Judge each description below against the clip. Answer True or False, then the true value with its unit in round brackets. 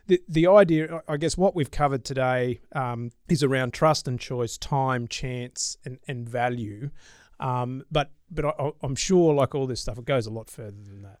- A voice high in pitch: False (135 Hz)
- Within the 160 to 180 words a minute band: False (200 wpm)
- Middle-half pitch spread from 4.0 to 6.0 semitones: False (3.6 semitones)